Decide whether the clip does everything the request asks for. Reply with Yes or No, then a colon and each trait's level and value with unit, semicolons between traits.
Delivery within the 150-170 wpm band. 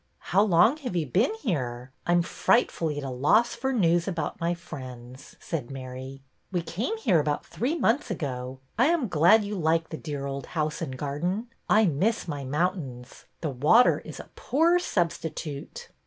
No: average, 180 wpm